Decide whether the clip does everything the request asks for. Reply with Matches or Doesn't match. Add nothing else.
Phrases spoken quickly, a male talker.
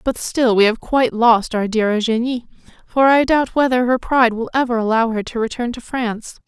Doesn't match